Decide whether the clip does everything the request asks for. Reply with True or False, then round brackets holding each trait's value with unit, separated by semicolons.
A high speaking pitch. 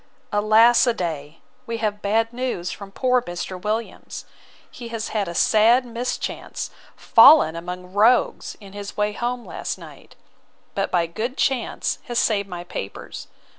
True (215 Hz)